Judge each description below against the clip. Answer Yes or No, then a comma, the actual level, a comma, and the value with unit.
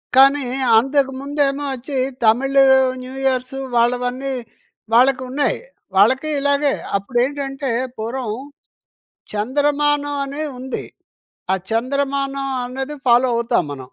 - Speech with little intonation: Yes, narrow, 2.3 semitones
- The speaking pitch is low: No, very high, 265 Hz